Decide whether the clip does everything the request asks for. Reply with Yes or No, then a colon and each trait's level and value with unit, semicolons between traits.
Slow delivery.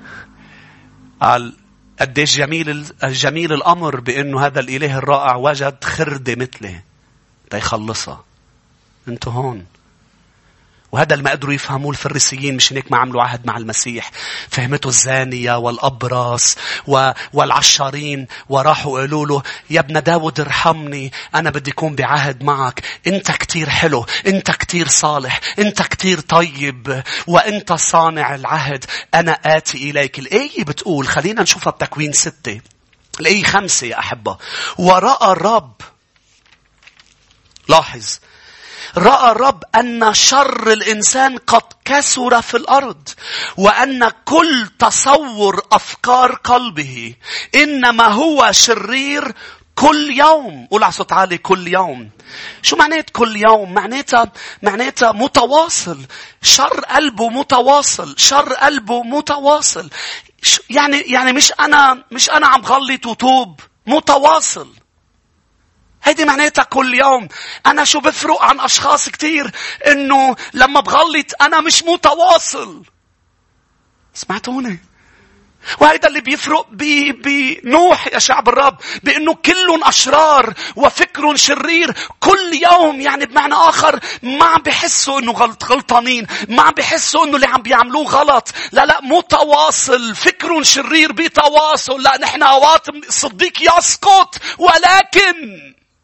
Yes: slow, 115 wpm